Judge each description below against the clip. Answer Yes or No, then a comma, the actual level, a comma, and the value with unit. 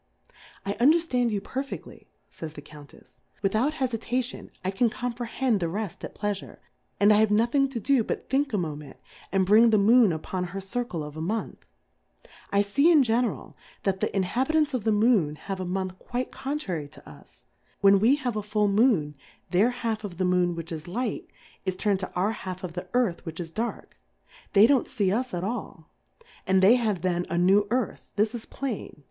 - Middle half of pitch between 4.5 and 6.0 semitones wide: Yes, average, 4.9 semitones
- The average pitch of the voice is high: Yes, high, 210 Hz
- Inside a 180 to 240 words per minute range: Yes, average, 195 wpm